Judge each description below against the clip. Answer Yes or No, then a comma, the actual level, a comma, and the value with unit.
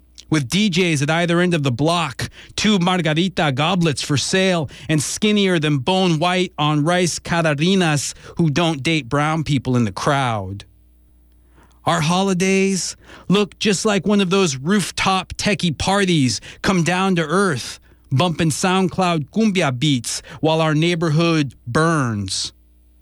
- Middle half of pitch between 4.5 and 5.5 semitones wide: Yes, average, 5.1 semitones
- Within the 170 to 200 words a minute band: No, slow, 135 wpm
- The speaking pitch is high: No, medium, 165 Hz